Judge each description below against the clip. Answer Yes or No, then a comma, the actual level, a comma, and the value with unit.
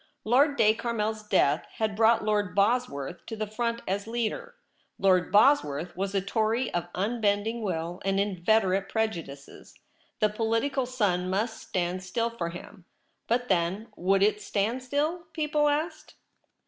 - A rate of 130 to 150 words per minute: Yes, average, 145 wpm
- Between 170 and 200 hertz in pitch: No, high, 215 Hz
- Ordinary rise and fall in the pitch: Yes, average, 3.9 semitones